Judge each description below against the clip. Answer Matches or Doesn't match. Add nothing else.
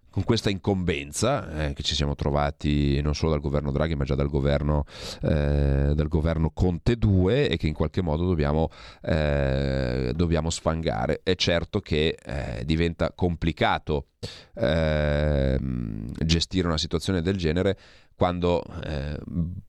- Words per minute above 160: Doesn't match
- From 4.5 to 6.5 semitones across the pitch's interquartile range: Doesn't match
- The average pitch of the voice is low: Matches